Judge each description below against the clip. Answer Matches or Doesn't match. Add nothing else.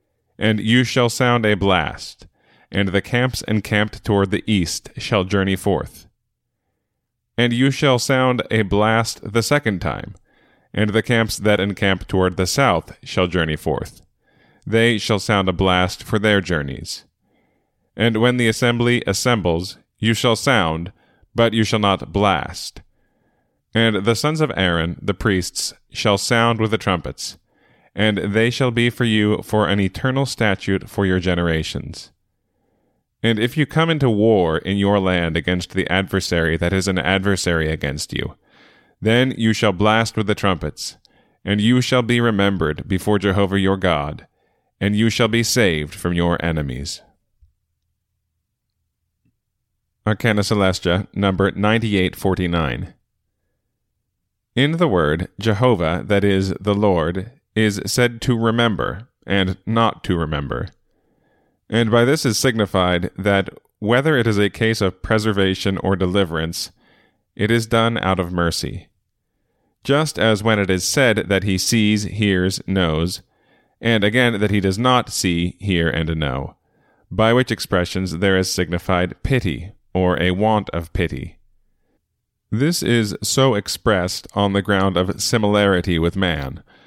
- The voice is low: Matches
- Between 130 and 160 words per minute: Matches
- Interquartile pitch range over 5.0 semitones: Doesn't match